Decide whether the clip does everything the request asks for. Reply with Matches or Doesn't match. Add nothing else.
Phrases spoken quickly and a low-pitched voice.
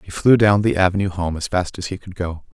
Matches